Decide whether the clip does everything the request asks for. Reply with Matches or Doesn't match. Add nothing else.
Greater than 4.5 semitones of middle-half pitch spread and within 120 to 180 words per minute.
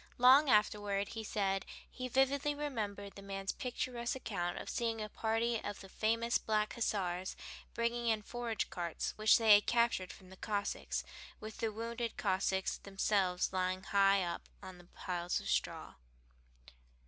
Doesn't match